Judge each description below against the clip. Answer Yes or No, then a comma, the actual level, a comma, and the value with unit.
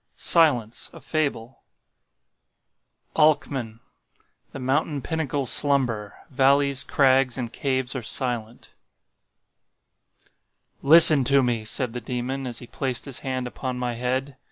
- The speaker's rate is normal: No, slow, 105 wpm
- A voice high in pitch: No, low, 130 Hz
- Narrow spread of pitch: Yes, narrow, 2.3 semitones